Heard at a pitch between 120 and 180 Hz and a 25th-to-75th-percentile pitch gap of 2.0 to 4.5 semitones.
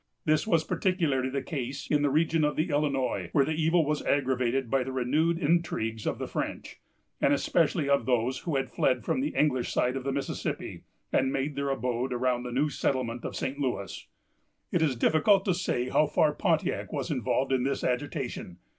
Yes: medium, 140 Hz; average, 3.3 semitones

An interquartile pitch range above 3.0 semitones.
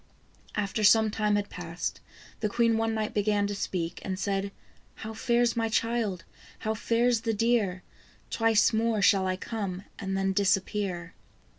No: average, 2.7 semitones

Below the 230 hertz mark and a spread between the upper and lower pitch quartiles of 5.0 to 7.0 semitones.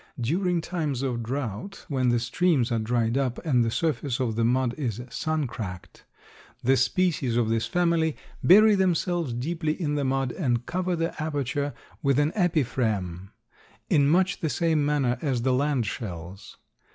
Yes: low, 135 Hz; average, 5.3 semitones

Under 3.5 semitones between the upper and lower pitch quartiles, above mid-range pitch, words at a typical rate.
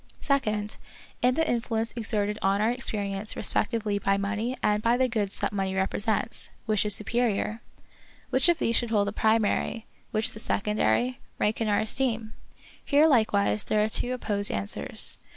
Yes: narrow, 2.5 semitones; high, 215 Hz; average, 170 wpm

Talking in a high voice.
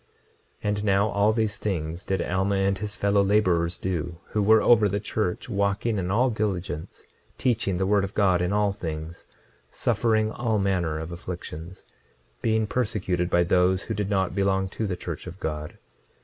No: very low, 95 Hz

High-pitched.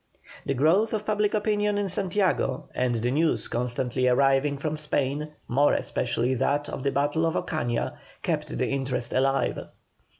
No: medium, 140 Hz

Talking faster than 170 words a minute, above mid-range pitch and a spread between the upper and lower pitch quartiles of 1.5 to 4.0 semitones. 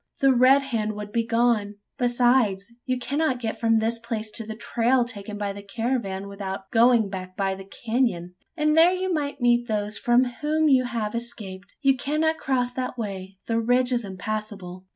Yes: average, 185 wpm; high, 230 Hz; average, 3.7 semitones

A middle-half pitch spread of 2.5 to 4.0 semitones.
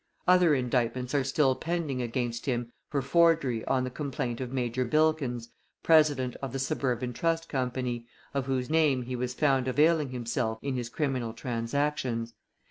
Yes: average, 3.1 semitones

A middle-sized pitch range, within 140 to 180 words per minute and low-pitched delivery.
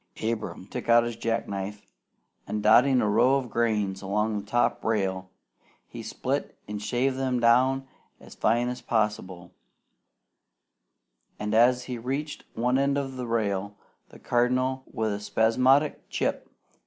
Yes: average, 3.4 semitones; average, 145 wpm; low, 115 Hz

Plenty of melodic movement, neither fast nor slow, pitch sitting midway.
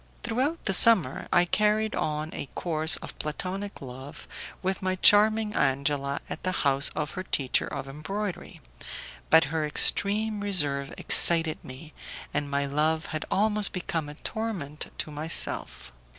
Yes: wide, 5.9 semitones; average, 145 wpm; medium, 160 Hz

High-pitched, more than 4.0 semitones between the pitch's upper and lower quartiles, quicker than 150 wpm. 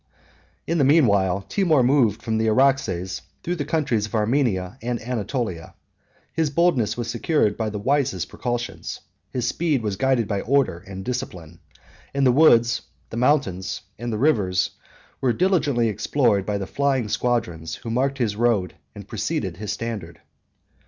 No: low, 120 Hz; average, 5.2 semitones; average, 160 wpm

